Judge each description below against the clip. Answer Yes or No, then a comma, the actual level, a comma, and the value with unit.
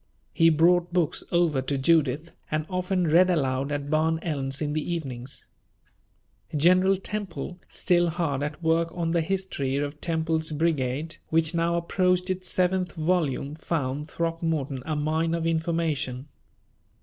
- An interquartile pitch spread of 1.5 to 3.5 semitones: Yes, average, 2.9 semitones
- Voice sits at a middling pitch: Yes, medium, 165 Hz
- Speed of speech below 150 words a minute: Yes, average, 140 wpm